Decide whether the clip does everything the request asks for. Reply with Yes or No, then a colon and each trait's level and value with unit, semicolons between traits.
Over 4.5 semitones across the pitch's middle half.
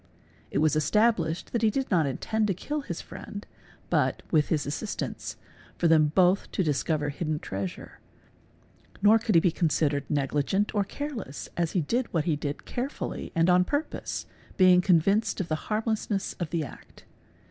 Yes: wide, 5.5 semitones